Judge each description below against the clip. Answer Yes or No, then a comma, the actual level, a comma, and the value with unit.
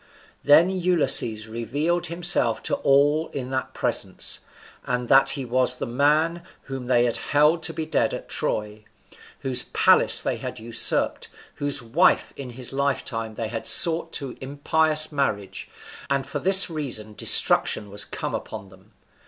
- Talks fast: No, average, 155 wpm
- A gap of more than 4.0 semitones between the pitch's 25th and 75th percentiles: Yes, average, 5.1 semitones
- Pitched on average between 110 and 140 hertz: Yes, low, 135 Hz